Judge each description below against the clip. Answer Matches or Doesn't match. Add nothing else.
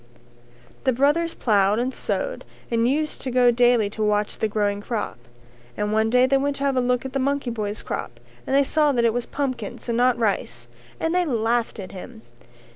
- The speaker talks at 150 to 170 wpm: Doesn't match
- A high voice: Matches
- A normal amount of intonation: Matches